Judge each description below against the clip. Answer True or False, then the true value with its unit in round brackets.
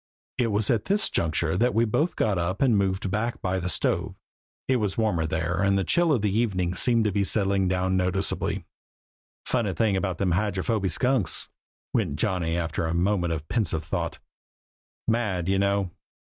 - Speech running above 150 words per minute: True (175 wpm)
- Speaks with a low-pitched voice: True (95 Hz)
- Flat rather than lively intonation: False (3.5 semitones)